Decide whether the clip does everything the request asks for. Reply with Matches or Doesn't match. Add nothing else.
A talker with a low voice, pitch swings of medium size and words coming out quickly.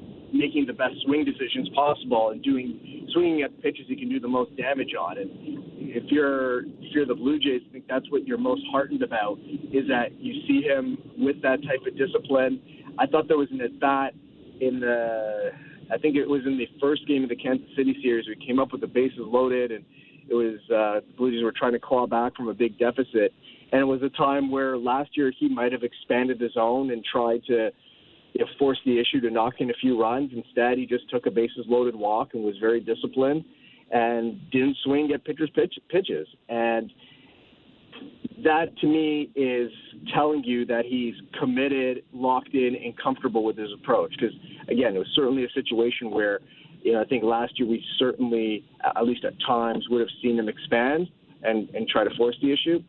Matches